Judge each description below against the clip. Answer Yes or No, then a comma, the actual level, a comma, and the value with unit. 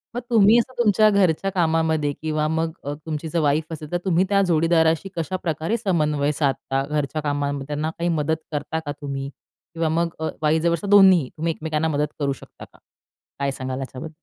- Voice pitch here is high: No, medium, 160 Hz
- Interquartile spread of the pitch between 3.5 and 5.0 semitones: No, narrow, 2.6 semitones